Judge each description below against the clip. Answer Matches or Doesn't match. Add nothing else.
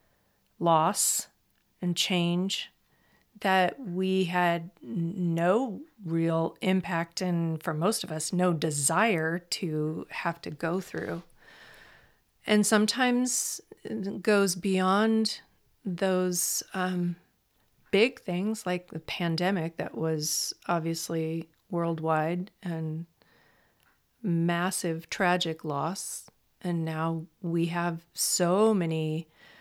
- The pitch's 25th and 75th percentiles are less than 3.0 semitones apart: Matches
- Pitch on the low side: Doesn't match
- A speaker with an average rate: Doesn't match